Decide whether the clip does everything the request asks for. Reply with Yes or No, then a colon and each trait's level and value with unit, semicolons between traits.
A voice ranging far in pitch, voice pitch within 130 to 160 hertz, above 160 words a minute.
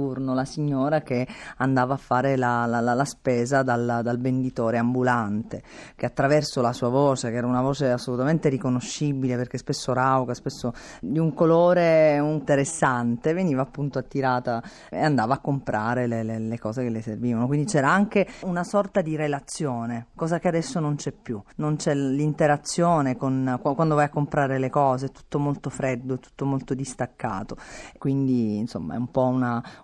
No: average, 3.2 semitones; low, 135 Hz; fast, 170 wpm